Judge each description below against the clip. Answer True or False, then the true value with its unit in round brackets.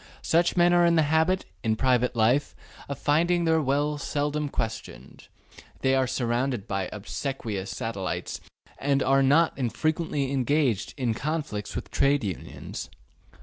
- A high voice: False (135 Hz)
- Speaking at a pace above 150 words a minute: False (140 wpm)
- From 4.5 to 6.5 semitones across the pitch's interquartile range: True (4.8 semitones)